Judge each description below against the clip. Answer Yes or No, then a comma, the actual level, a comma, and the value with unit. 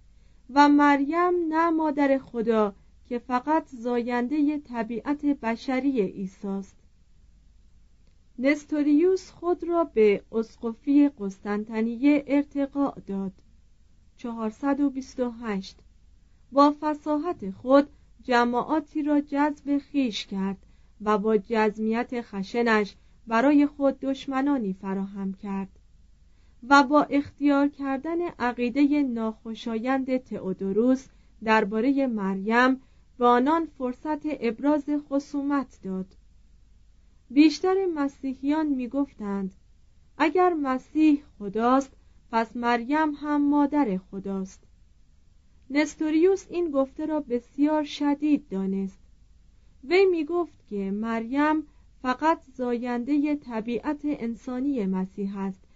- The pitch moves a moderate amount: No, wide, 5.9 semitones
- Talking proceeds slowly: Yes, slow, 90 wpm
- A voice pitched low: No, very high, 255 Hz